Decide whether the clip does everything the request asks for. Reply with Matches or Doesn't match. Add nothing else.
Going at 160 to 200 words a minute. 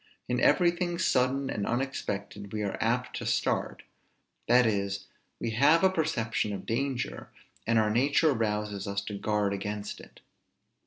Doesn't match